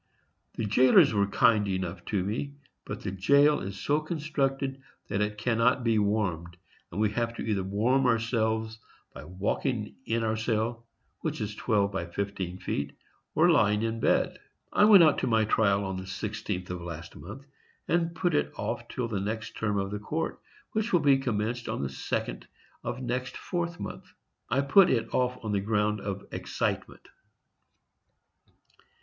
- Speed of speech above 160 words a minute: Yes, average, 175 wpm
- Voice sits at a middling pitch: No, low, 110 Hz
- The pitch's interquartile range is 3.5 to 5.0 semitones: Yes, average, 4.2 semitones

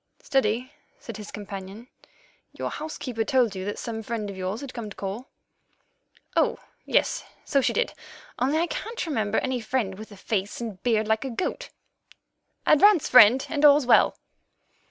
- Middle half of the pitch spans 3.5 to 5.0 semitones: Yes, average, 4.4 semitones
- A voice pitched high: Yes, high, 230 Hz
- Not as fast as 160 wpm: No, average, 165 wpm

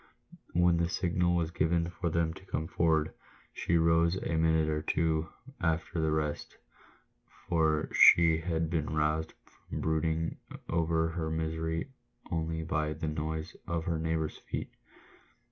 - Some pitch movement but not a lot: No, narrow, 0.9 semitones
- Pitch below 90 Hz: Yes, very low, 80 Hz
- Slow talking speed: No, average, 145 wpm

